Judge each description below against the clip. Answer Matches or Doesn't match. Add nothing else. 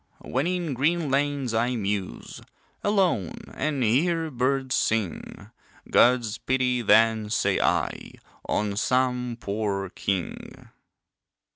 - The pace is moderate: Doesn't match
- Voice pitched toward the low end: Matches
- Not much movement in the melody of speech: Doesn't match